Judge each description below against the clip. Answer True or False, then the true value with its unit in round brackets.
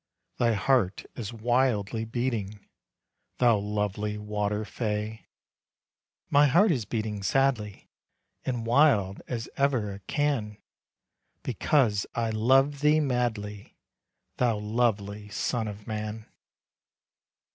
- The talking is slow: True (105 wpm)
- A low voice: True (110 Hz)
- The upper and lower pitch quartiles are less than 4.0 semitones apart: True (3.2 semitones)